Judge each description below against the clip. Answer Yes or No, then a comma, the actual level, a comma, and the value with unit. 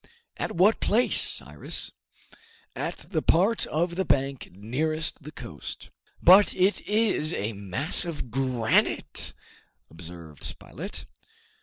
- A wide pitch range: Yes, wide, 8.6 semitones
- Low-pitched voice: No, medium, 155 Hz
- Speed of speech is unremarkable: No, slow, 115 wpm